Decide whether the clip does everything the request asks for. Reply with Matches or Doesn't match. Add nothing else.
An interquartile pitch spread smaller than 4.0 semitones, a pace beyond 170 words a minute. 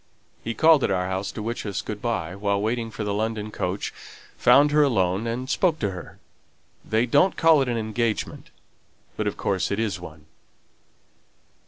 Matches